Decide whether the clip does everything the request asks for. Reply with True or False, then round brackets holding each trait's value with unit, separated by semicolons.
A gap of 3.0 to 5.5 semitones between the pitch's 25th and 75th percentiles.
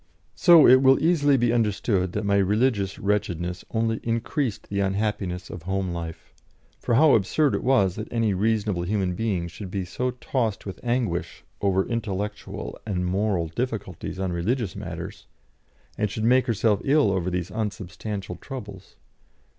True (3.8 semitones)